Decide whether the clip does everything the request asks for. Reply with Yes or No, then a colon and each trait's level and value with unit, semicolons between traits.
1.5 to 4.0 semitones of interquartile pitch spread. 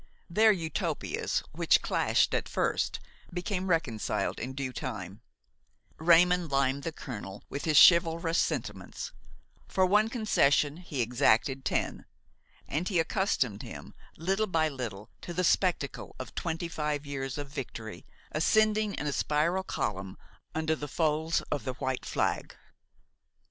No: average, 5.1 semitones